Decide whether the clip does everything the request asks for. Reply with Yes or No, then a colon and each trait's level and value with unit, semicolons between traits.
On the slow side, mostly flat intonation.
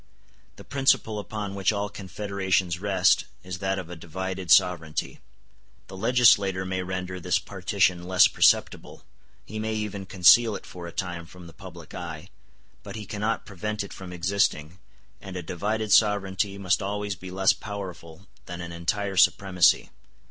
No: average, 155 wpm; narrow, 2.3 semitones